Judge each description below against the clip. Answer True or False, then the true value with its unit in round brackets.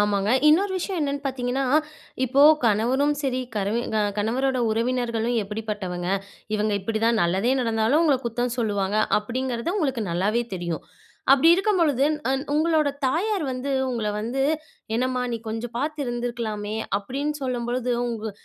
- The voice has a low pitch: False (240 Hz)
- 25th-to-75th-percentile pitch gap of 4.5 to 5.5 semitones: False (3.9 semitones)